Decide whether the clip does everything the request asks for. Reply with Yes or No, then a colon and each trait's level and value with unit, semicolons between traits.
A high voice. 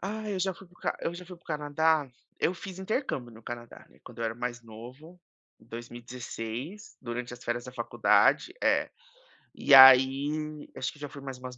No: low, 135 Hz